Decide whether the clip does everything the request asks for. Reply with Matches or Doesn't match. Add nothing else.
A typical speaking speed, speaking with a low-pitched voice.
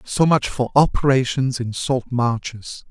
Matches